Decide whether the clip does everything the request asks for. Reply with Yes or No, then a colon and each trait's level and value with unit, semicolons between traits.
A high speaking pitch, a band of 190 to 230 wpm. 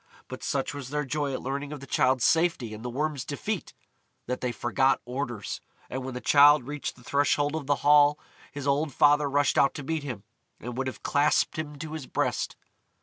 No: medium, 140 Hz; fast, 205 wpm